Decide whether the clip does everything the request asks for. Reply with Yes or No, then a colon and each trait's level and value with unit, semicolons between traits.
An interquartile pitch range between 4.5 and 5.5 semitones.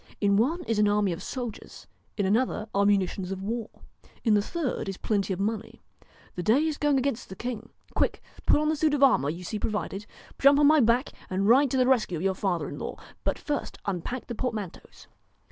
Yes: average, 5.0 semitones